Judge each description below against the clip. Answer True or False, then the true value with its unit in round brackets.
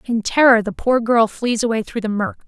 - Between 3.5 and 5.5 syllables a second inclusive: True (5.2 syllables/s)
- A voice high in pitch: True (230 Hz)